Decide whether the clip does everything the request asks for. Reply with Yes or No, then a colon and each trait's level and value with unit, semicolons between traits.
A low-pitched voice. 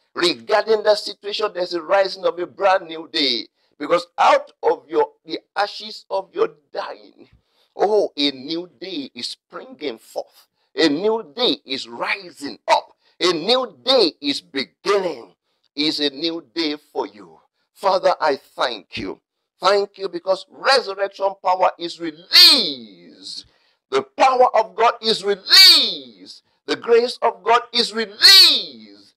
No: high, 200 Hz